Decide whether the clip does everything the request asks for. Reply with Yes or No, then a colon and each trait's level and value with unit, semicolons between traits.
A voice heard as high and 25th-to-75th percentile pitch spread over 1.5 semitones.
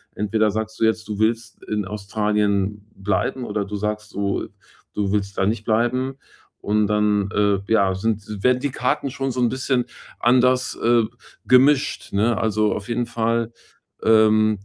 No: low, 110 Hz; narrow, 2.5 semitones